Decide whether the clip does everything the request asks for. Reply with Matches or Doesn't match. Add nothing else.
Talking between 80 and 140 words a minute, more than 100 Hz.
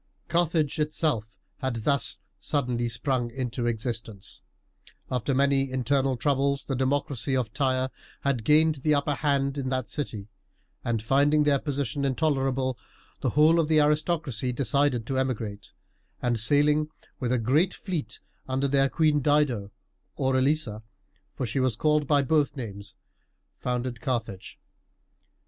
Matches